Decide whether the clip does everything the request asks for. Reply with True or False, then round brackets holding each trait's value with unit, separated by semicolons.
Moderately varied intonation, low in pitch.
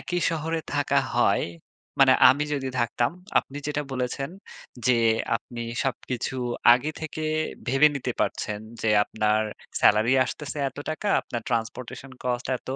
True (3.8 semitones; 130 Hz)